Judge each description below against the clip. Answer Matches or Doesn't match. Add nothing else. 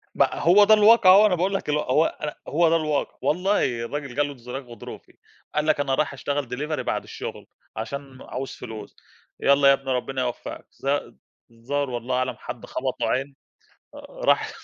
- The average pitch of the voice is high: Doesn't match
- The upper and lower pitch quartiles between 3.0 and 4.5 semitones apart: Matches